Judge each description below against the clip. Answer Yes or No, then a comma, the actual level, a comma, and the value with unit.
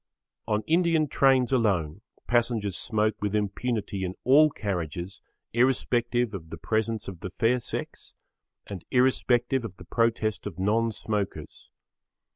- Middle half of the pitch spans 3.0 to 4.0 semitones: Yes, average, 3.7 semitones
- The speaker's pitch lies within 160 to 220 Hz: No, low, 110 Hz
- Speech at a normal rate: No, slow, 130 wpm